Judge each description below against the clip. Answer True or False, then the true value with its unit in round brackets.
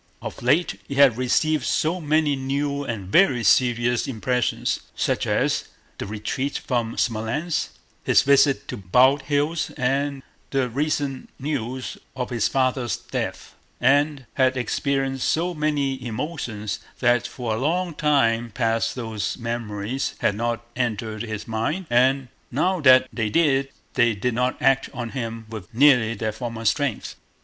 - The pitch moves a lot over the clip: False (3.6 semitones)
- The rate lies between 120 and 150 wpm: True (140 wpm)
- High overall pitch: False (130 Hz)